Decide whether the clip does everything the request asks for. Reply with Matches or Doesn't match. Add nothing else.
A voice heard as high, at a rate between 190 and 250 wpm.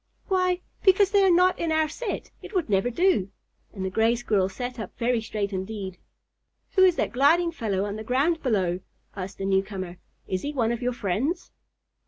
Matches